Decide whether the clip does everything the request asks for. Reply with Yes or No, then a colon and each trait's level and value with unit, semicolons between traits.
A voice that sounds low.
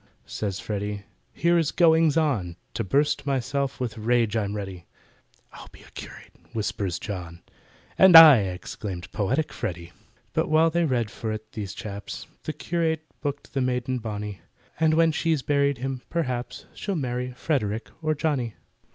Yes: low, 125 Hz